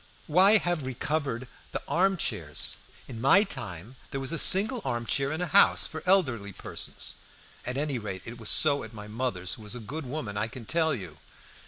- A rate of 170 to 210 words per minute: Yes, average, 200 wpm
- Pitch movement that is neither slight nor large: No, wide, 6.2 semitones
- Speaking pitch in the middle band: No, low, 130 Hz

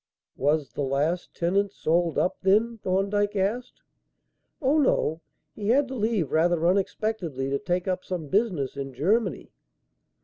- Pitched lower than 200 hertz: Yes, medium, 185 Hz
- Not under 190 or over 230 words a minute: No, average, 140 wpm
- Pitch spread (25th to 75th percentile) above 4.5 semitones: Yes, average, 5.0 semitones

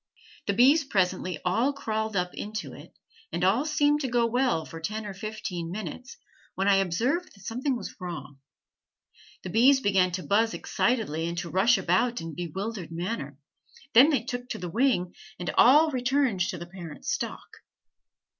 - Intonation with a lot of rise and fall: Yes, wide, 5.7 semitones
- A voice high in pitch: Yes, high, 210 Hz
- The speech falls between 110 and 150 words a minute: No, average, 175 wpm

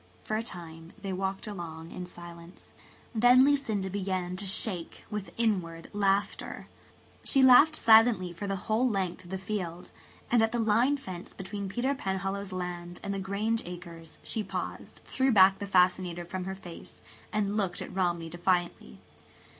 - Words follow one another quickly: No, average, 160 wpm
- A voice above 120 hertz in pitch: Yes, high, 190 Hz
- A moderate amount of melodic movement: Yes, average, 3.4 semitones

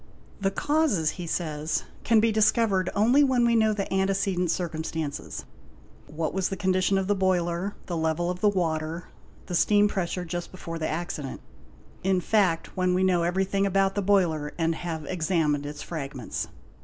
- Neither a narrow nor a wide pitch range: Yes, average, 3.2 semitones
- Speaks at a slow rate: No, average, 165 wpm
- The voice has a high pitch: No, medium, 180 Hz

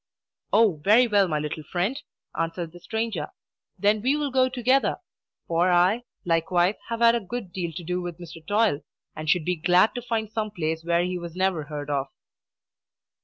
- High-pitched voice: No, medium, 180 Hz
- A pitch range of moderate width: Yes, average, 5.0 semitones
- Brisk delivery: No, average, 185 wpm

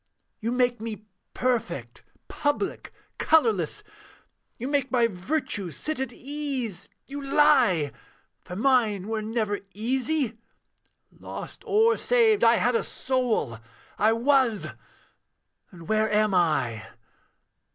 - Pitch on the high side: Yes, high, 230 Hz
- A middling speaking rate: No, slow, 110 wpm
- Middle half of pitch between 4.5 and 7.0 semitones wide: Yes, average, 4.9 semitones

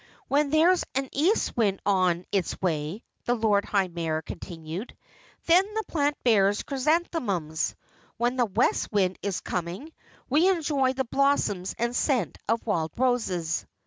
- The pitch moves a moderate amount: No, wide, 7.3 semitones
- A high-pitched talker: Yes, high, 225 Hz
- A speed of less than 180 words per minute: Yes, average, 145 wpm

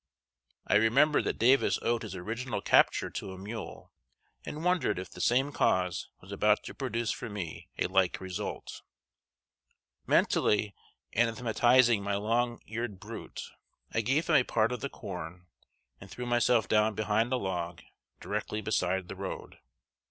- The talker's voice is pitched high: No, low, 110 Hz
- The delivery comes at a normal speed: Yes, average, 150 wpm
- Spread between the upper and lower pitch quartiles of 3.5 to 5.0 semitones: Yes, average, 4.1 semitones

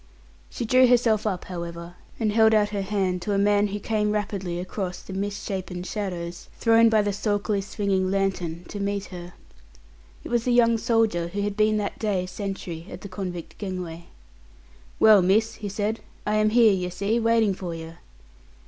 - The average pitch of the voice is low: No, high, 200 Hz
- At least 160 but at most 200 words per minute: Yes, average, 180 wpm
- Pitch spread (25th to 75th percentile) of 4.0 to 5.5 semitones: No, average, 2.9 semitones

